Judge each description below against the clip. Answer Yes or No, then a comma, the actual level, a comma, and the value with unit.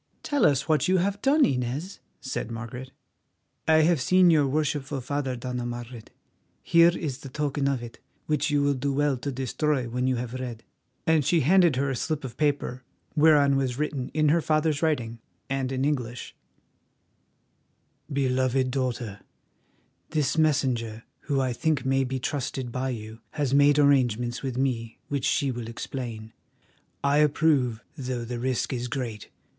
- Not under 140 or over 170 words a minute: Yes, average, 160 wpm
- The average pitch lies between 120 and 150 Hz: Yes, low, 135 Hz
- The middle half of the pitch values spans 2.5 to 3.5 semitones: Yes, average, 3.2 semitones